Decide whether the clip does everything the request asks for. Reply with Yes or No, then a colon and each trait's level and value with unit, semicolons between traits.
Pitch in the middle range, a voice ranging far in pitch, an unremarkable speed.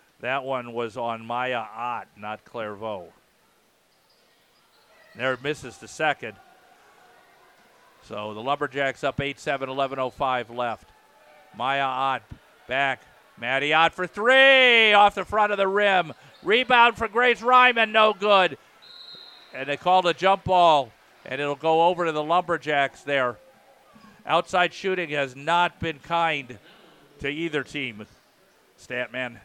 No: medium, 145 Hz; wide, 6.2 semitones; slow, 130 wpm